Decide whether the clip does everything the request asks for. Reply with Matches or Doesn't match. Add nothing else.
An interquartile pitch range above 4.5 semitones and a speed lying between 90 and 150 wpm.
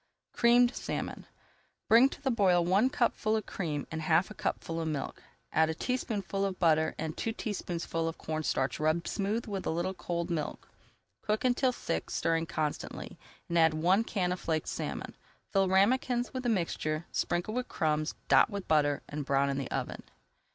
Doesn't match